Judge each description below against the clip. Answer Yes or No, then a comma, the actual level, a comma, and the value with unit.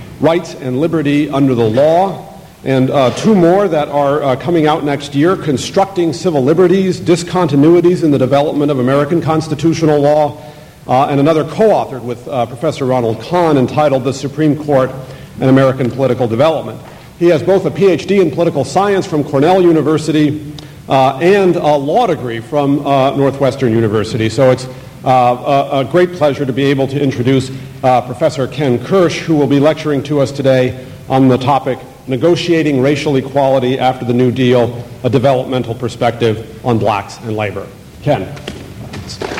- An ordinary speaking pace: Yes, average, 160 wpm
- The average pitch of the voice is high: No, medium, 140 Hz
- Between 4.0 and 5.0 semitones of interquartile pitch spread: No, average, 3.5 semitones